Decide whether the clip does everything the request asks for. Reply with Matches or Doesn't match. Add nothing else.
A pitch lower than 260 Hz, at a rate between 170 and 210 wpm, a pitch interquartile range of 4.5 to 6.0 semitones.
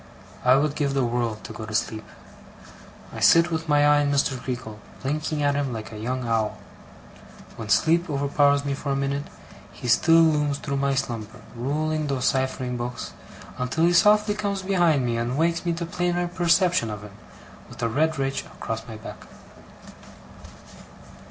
Matches